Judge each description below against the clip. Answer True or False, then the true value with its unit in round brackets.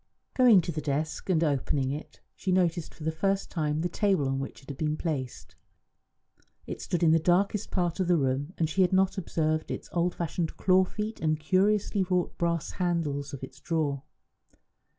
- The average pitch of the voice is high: False (165 Hz)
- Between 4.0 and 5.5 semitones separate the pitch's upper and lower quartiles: False (3.5 semitones)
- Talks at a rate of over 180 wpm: True (195 wpm)